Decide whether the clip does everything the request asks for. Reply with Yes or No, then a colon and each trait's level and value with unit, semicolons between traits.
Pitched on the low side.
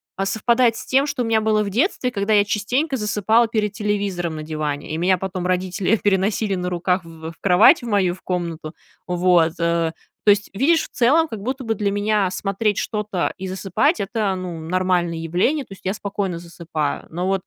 No: high, 195 Hz